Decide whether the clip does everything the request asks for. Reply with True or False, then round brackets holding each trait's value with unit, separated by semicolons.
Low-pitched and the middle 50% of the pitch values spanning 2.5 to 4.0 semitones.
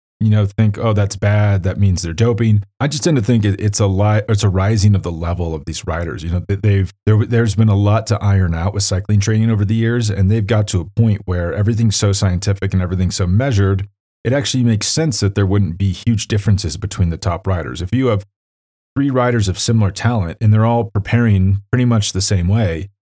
True (100 Hz; 2.8 semitones)